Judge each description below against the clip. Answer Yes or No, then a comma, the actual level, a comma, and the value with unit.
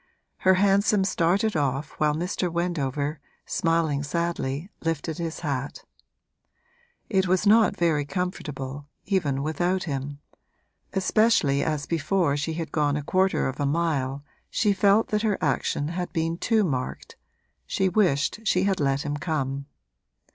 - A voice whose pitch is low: No, medium, 165 Hz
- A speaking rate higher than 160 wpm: No, average, 140 wpm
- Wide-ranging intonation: No, average, 4.6 semitones